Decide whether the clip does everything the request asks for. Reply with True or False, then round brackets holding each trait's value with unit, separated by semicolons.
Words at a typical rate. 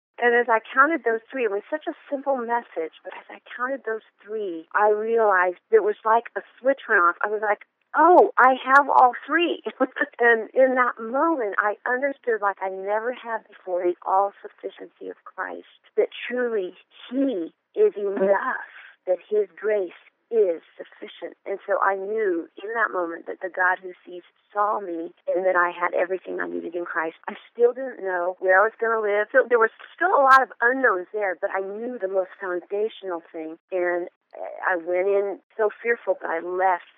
True (195 wpm)